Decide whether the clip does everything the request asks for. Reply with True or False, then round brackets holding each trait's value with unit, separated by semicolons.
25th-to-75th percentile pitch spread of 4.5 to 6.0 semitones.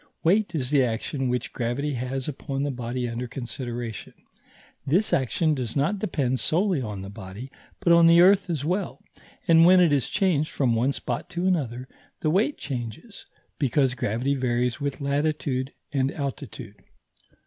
True (4.9 semitones)